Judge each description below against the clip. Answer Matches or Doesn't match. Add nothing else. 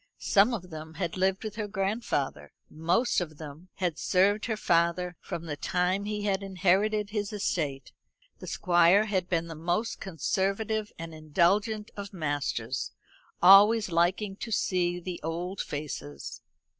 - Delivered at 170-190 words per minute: Doesn't match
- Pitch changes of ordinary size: Matches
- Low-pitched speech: Doesn't match